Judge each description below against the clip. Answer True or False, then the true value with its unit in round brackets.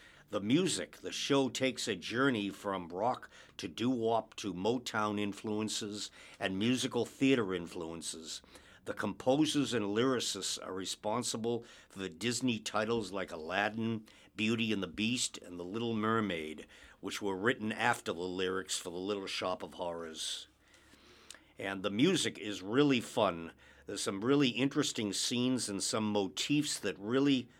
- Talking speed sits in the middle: True (145 wpm)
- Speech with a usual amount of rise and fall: True (4.3 semitones)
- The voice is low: True (110 Hz)